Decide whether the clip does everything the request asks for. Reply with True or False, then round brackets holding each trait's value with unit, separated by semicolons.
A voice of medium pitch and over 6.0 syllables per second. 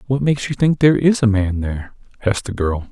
False (115 Hz; 6.4 syllables/s)